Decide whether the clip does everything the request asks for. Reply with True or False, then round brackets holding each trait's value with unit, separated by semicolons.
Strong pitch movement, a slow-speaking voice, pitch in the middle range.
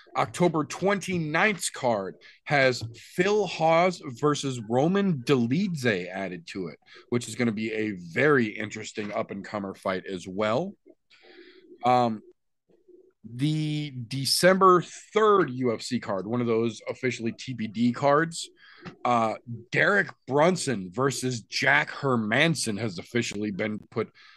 False (7.6 semitones; 120 wpm; 130 Hz)